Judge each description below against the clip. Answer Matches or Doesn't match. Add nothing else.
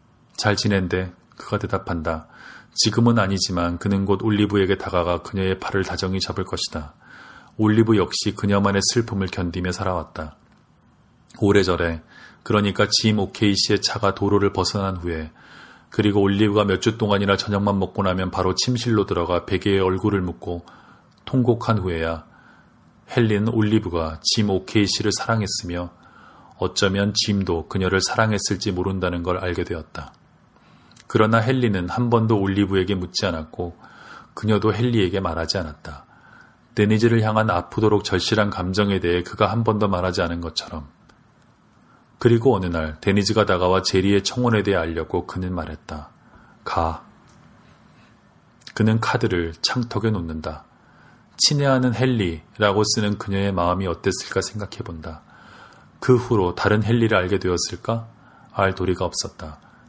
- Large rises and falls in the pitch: Doesn't match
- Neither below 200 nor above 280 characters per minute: Doesn't match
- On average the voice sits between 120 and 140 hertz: Doesn't match